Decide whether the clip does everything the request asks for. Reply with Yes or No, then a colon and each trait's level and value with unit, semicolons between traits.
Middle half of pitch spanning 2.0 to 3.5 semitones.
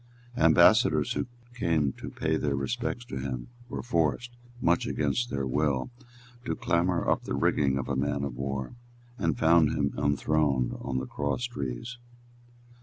No: average, 3.9 semitones